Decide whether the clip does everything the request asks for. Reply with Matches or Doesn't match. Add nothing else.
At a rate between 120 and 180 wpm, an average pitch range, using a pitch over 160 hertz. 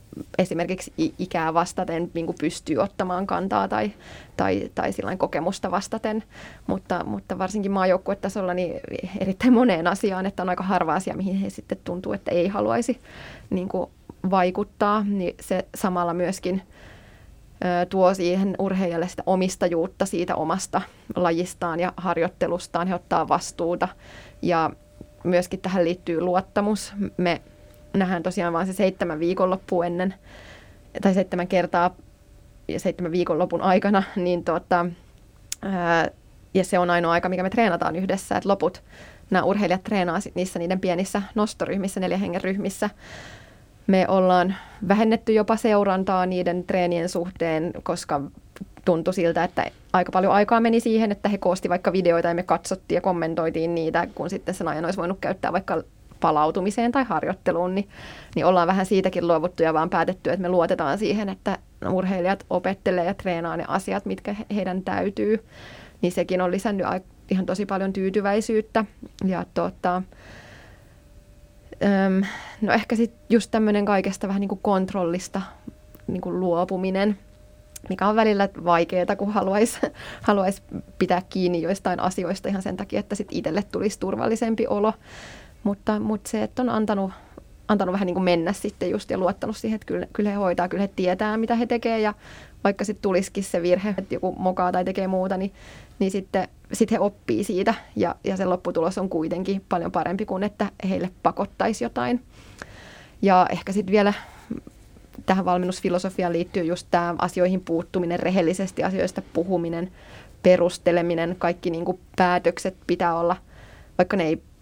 Doesn't match